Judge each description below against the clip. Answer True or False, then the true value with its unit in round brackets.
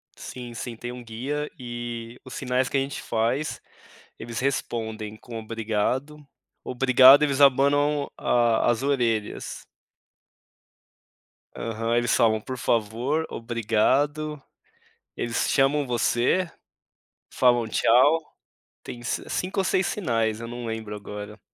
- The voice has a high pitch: False (120 Hz)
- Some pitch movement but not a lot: True (3.3 semitones)